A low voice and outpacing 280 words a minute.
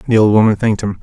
Yes: low, 105 Hz; fast, 295 wpm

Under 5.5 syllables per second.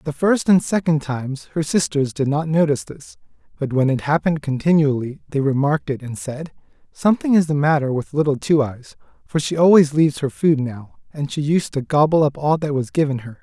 No: 5.6 syllables/s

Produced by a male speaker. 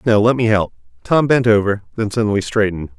Yes: male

